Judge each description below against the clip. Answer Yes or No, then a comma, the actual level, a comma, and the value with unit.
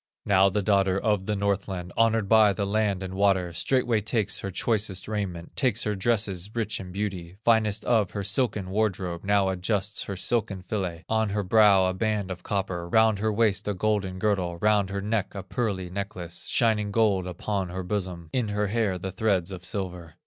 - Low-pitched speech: Yes, low, 100 Hz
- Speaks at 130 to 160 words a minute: No, average, 190 wpm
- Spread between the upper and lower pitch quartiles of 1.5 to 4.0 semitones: Yes, narrow, 2.4 semitones